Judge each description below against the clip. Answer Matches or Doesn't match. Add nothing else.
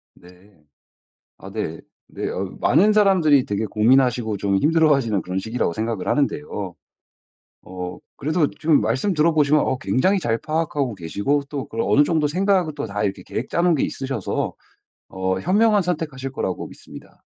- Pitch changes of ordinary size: Doesn't match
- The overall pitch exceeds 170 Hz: Doesn't match